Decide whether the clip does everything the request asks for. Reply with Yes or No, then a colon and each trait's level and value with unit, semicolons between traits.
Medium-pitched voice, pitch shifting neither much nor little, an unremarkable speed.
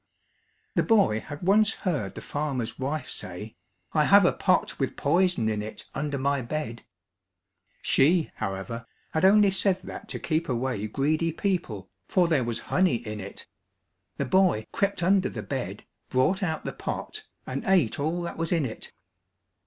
No: medium, 150 Hz; wide, 7.7 semitones; average, 165 wpm